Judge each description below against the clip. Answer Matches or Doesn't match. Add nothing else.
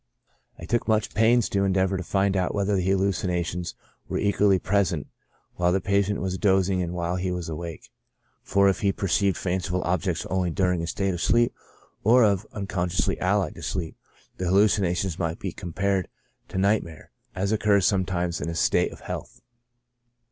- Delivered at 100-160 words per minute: Doesn't match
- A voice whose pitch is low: Matches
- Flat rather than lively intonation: Matches